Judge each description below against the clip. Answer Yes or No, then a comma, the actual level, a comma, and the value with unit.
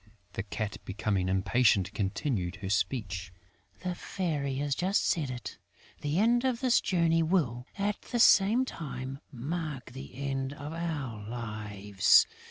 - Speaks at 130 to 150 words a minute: Yes, average, 140 wpm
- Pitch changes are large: Yes, wide, 8.0 semitones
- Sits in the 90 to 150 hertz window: Yes, low, 135 Hz